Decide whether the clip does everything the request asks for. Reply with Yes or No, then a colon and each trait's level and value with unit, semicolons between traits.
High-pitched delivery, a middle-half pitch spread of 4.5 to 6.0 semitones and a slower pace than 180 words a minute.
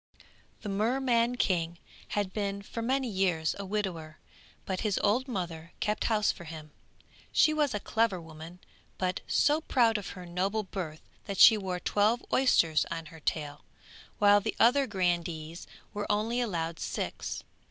Yes: high, 200 Hz; average, 4.8 semitones; average, 155 wpm